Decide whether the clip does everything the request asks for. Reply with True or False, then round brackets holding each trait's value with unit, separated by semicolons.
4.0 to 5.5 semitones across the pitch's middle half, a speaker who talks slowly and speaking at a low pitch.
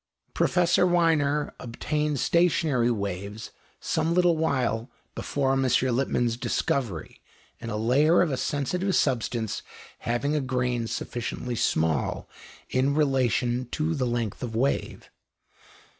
True (4.3 semitones; 115 wpm; 130 Hz)